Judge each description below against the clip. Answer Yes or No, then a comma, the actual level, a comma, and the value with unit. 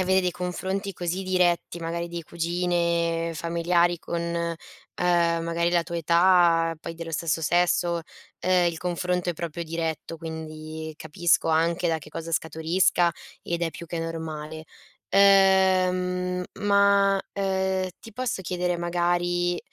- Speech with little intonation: Yes, narrow, 1.6 semitones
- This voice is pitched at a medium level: Yes, medium, 170 Hz